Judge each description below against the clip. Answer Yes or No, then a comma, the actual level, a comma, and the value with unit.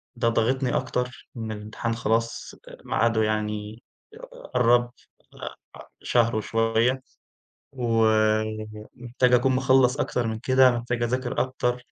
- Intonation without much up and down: Yes, narrow, 2.1 semitones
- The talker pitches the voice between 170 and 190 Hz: No, low, 120 Hz